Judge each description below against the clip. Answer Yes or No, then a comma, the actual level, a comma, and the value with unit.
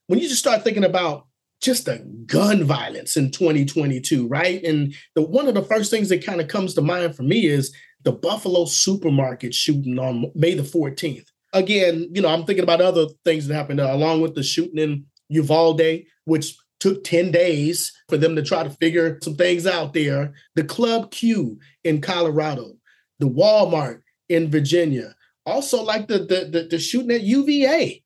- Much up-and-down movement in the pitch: No, average, 3.5 semitones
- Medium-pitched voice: Yes, medium, 165 Hz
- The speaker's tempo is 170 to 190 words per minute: Yes, average, 180 wpm